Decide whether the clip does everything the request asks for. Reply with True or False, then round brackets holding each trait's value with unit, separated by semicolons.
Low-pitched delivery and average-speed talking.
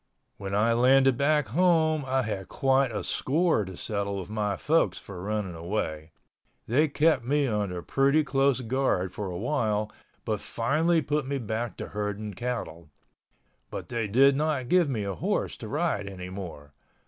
True (115 Hz; 160 wpm)